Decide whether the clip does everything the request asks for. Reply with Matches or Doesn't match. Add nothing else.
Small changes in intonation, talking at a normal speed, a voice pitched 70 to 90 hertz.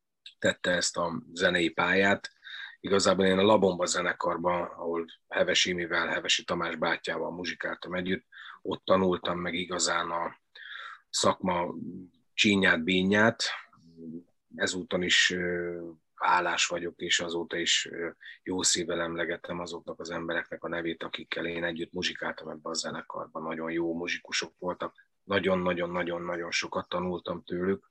Matches